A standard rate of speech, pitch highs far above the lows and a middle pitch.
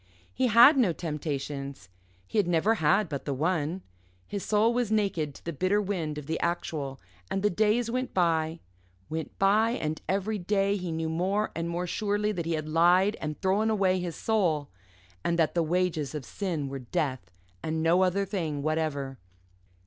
No: average, 180 wpm; average, 4.6 semitones; medium, 175 Hz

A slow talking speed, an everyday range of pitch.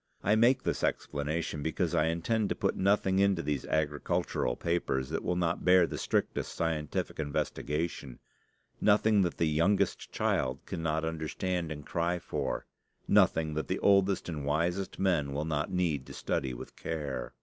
No: average, 160 wpm; average, 3.7 semitones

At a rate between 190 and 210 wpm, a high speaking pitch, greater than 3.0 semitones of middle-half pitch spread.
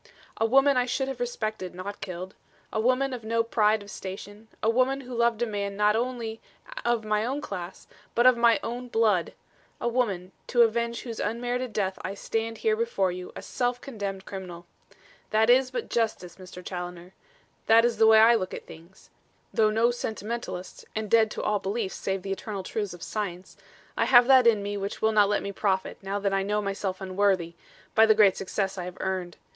Yes: fast, 205 wpm; high, 215 Hz; average, 3.5 semitones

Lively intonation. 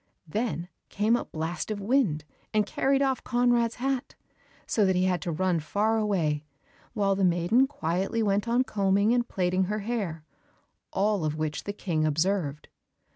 No: average, 5.0 semitones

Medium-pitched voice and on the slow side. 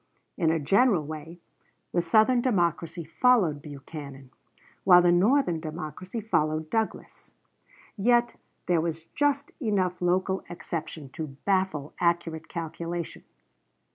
Yes: medium, 170 Hz; slow, 110 wpm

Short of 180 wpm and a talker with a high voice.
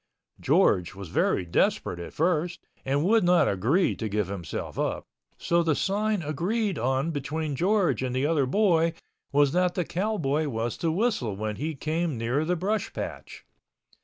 No: average, 160 wpm; medium, 155 Hz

